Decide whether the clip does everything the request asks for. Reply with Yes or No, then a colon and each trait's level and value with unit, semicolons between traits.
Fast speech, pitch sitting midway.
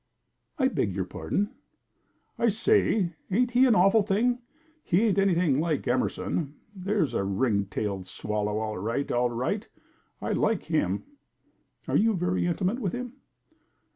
No: average, 145 wpm; medium, 175 Hz